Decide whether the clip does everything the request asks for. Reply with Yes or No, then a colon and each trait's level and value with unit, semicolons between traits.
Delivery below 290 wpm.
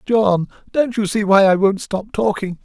Yes: fast, 205 wpm